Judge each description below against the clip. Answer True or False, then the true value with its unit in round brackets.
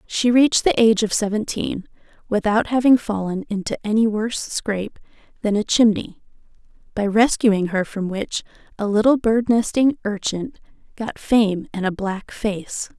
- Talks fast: False (150 wpm)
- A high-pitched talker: True (215 Hz)